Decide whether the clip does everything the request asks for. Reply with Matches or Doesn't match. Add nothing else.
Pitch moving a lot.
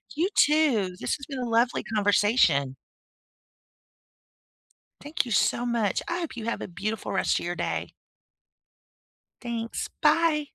Matches